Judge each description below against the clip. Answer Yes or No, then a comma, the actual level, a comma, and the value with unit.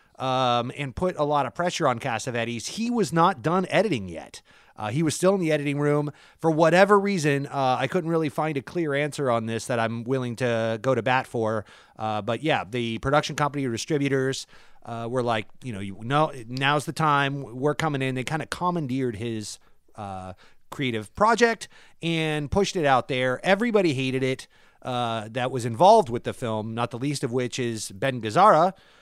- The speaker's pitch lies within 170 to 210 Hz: No, low, 135 Hz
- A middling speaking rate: Yes, average, 195 wpm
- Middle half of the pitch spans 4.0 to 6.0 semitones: Yes, average, 4.6 semitones